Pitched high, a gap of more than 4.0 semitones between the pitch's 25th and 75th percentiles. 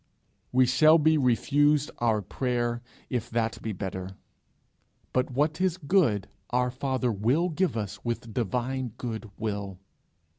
No: low, 125 Hz; average, 4.4 semitones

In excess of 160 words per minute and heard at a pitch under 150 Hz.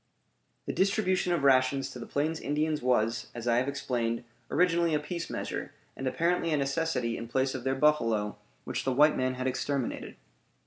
Yes: average, 180 wpm; low, 135 Hz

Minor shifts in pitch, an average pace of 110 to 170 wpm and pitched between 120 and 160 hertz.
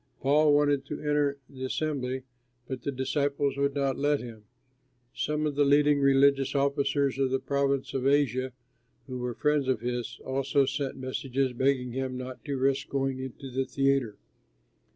Yes: narrow, 1.5 semitones; average, 165 wpm; low, 135 Hz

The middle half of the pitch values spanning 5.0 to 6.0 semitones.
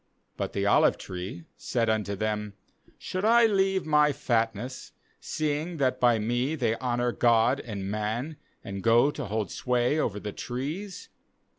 Yes: wide, 5.5 semitones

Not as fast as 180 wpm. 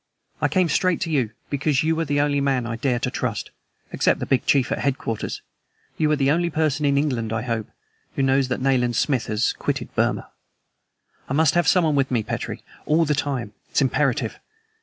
No: average, 200 wpm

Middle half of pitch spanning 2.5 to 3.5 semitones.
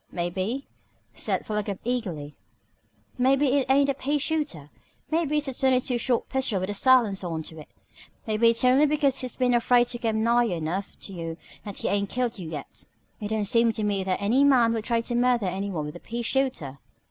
No: average, 5.1 semitones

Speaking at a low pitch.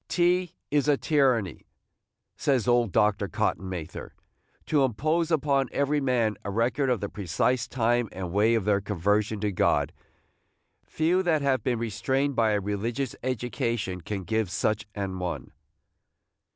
Yes: low, 115 Hz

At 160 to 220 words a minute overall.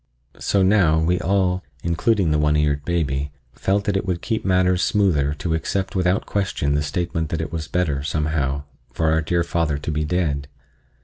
Yes: average, 175 wpm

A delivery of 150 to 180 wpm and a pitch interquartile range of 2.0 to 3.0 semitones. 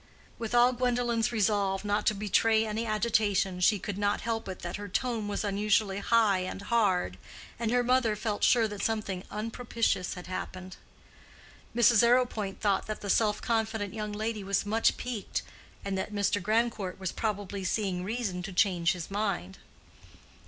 Yes: average, 165 wpm; average, 2.7 semitones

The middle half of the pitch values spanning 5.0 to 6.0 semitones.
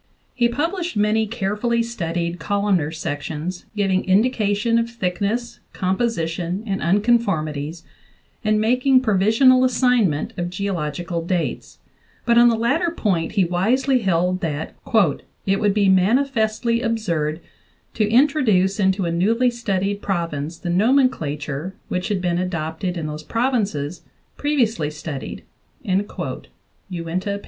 Yes: average, 5.3 semitones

